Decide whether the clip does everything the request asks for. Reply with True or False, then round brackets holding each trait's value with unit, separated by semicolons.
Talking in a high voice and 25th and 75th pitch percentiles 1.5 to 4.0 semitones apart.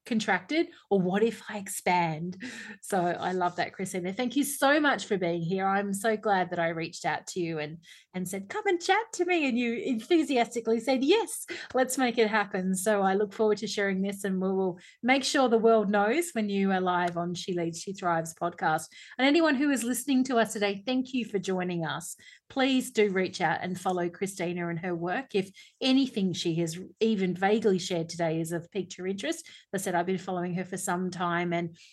False (195 Hz; 4.8 semitones)